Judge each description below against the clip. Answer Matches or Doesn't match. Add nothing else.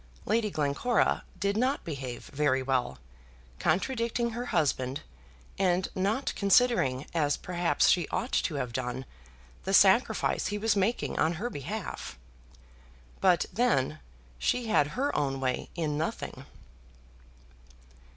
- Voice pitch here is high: Doesn't match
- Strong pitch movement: Matches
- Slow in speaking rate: Matches